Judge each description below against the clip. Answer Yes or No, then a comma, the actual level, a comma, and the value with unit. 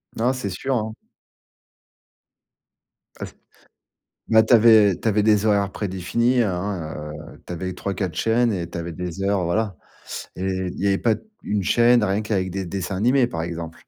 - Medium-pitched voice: No, low, 100 Hz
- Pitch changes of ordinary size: Yes, average, 3.7 semitones